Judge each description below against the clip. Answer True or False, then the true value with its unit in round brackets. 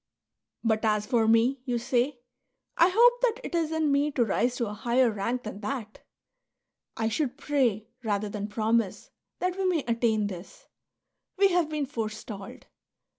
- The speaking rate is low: False (180 wpm)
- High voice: True (240 Hz)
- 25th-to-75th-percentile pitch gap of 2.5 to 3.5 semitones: False (5.3 semitones)